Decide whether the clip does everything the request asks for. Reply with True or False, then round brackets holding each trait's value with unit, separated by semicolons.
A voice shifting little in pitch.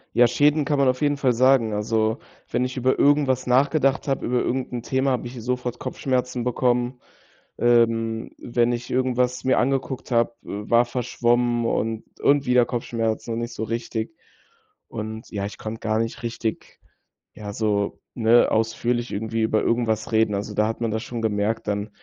True (2.1 semitones)